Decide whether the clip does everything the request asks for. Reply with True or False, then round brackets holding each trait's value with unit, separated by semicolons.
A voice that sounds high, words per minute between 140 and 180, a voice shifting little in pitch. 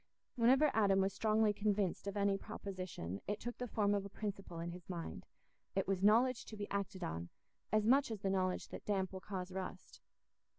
False (200 Hz; 200 wpm; 2.3 semitones)